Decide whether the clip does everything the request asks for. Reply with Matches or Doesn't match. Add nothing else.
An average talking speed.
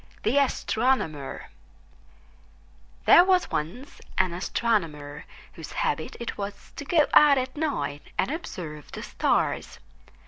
Doesn't match